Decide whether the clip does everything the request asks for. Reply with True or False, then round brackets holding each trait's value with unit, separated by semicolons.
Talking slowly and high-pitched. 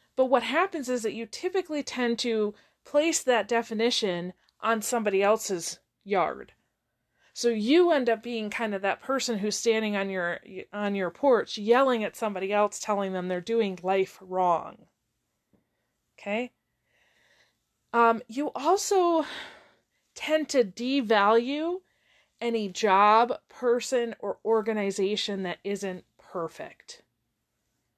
True (120 wpm; 225 Hz)